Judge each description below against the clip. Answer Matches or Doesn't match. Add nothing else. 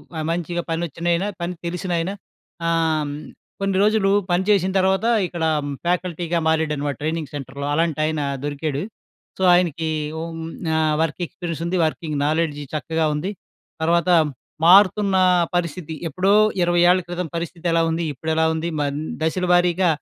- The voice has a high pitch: Doesn't match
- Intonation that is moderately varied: Doesn't match